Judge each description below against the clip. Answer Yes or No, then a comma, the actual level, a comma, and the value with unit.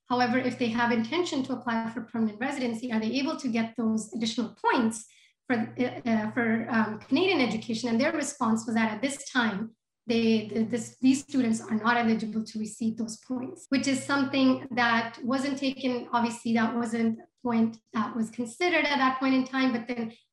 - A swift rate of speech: No, average, 190 wpm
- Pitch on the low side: No, high, 240 Hz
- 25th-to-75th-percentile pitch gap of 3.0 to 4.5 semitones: No, narrow, 2.4 semitones